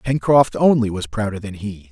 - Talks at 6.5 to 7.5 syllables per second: No, 5.0 syllables/s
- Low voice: Yes, low, 110 Hz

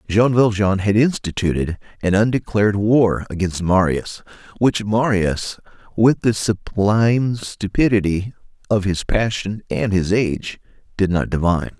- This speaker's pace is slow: Yes, slow, 120 wpm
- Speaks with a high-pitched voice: No, low, 105 Hz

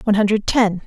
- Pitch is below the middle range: No, high, 210 Hz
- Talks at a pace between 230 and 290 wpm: No, fast, 210 wpm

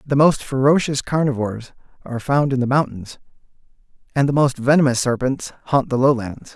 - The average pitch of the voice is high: No, low, 135 Hz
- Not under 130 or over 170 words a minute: Yes, average, 155 wpm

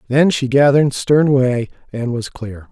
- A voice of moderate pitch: No, low, 130 Hz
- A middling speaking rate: Yes, average, 175 wpm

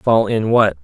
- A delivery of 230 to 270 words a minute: No, fast, 215 wpm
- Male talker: Yes, male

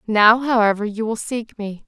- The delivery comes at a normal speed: Yes, average, 190 wpm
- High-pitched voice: Yes, high, 220 Hz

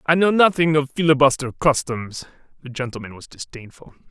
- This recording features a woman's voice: No, male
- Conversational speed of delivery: Yes, average, 145 wpm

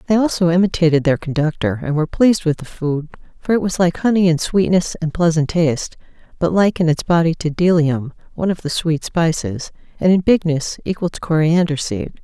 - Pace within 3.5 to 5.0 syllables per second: No, 5.6 syllables/s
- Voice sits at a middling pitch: Yes, medium, 165 Hz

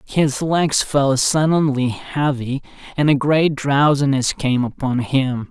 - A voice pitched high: No, medium, 140 Hz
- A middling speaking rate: No, slow, 130 wpm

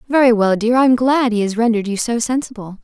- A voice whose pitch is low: No, high, 230 Hz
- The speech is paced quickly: Yes, fast, 255 wpm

